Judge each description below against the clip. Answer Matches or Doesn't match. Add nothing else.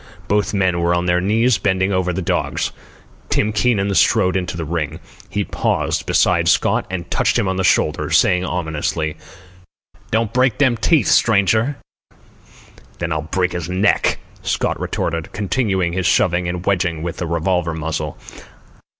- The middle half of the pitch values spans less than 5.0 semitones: Matches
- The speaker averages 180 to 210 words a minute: Doesn't match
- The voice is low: Matches